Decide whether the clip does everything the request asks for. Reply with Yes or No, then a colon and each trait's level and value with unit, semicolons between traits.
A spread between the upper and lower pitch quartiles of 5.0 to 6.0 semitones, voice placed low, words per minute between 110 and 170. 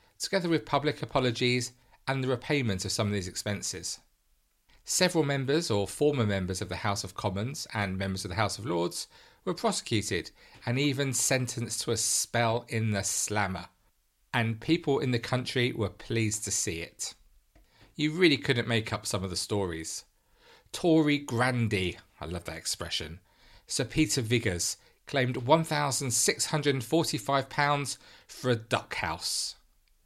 Yes: wide, 5.6 semitones; low, 120 Hz; average, 160 wpm